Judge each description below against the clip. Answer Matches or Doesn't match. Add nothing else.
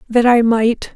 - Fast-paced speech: Doesn't match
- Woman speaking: Matches